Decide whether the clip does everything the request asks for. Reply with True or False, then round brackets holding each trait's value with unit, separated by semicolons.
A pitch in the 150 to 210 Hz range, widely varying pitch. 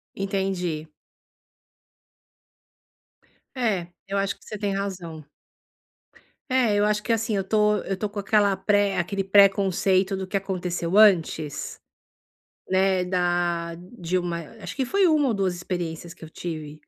False (190 Hz; 2.7 semitones)